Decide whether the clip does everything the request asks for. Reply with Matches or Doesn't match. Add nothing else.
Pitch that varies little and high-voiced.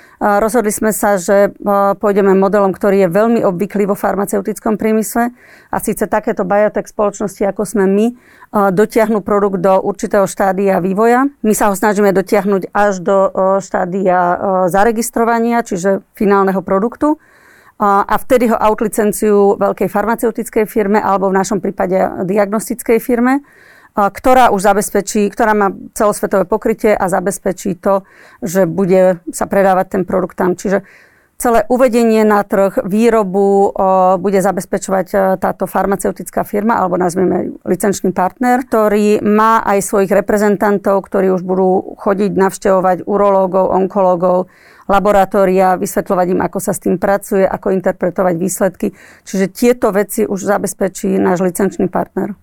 Matches